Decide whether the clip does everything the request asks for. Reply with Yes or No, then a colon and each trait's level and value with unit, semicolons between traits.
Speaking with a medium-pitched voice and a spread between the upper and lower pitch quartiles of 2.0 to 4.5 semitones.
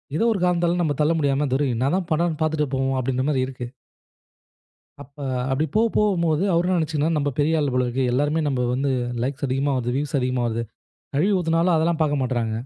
Yes: medium, 145 Hz; average, 3.7 semitones